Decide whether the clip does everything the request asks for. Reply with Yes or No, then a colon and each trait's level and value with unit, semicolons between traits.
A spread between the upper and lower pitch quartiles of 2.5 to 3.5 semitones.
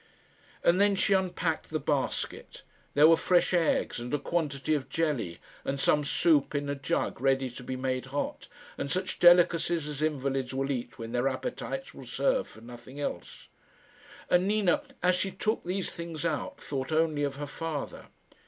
No: average, 4.4 semitones